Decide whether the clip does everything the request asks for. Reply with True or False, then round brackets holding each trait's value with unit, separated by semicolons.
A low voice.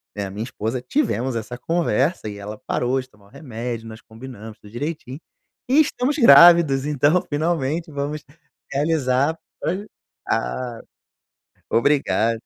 True (130 Hz)